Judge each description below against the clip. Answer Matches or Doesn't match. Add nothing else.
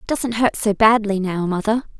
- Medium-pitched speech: Doesn't match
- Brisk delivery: Matches